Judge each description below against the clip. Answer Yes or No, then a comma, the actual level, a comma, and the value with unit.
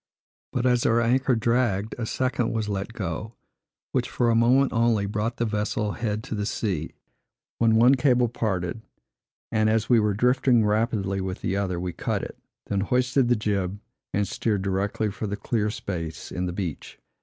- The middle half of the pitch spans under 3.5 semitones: Yes, average, 3.0 semitones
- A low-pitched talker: Yes, low, 110 Hz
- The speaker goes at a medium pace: Yes, average, 180 wpm